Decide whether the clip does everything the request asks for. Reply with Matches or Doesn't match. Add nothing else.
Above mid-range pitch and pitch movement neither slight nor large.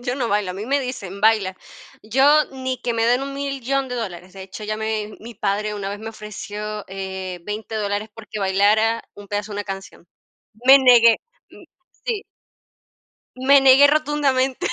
Matches